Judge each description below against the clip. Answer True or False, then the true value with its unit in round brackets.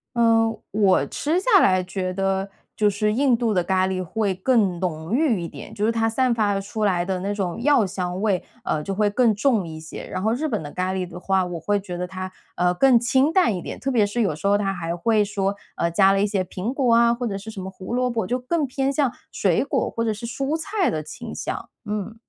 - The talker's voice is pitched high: True (205 Hz)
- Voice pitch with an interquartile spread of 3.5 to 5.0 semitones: True (4.1 semitones)